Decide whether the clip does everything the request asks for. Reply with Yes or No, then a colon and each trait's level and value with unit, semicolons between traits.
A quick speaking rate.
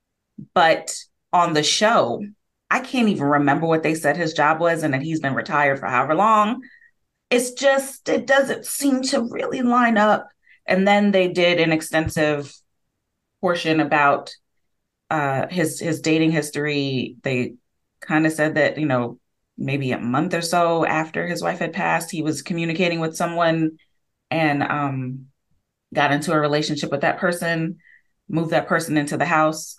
No: average, 165 wpm